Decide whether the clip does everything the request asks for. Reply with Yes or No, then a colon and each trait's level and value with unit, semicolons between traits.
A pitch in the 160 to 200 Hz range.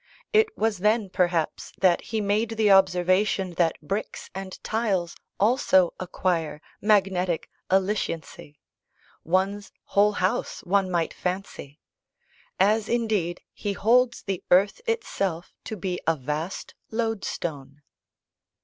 Yes: high, 190 Hz